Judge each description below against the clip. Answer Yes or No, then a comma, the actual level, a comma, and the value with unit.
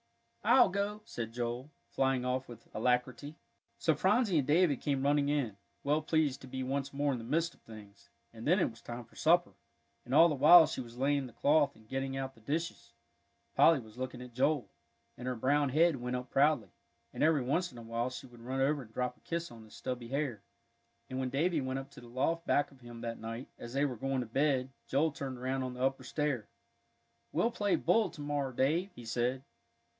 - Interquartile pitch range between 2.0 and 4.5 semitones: Yes, average, 3.3 semitones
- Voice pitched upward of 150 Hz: No, low, 135 Hz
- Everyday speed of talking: No, fast, 220 wpm